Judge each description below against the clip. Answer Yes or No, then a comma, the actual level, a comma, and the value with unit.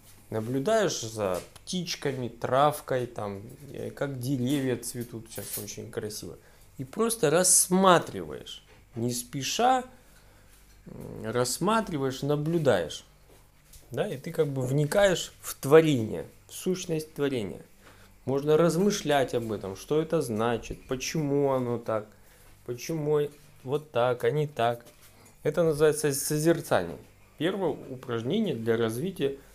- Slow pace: Yes, slow, 105 wpm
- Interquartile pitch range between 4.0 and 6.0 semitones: Yes, average, 5.2 semitones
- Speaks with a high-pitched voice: No, low, 135 Hz